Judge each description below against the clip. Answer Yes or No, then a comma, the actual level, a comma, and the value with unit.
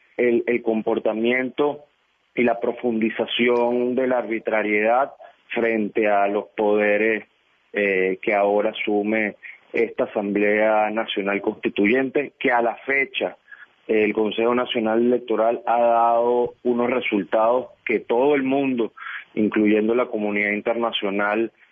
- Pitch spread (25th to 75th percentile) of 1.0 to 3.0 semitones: Yes, narrow, 2.5 semitones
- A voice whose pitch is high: No, low, 115 Hz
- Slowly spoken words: Yes, slow, 115 wpm